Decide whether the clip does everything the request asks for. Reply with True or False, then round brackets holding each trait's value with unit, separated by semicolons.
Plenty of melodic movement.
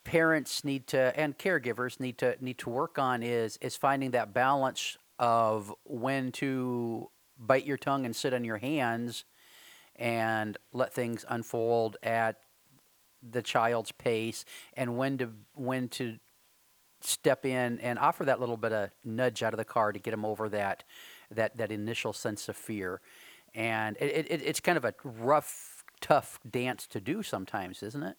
False (2.5 semitones)